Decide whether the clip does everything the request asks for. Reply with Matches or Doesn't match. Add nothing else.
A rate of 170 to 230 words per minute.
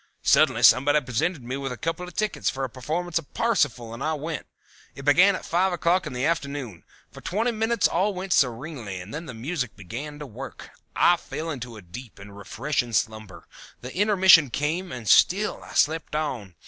Matches